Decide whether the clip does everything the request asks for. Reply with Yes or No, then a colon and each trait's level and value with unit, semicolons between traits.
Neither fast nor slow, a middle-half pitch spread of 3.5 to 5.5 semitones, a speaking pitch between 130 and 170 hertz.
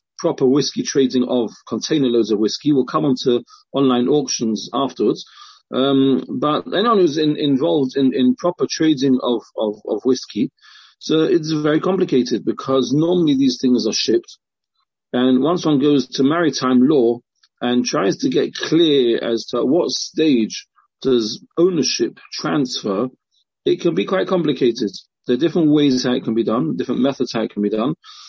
Yes: average, 165 wpm; average, 4.0 semitones; low, 135 Hz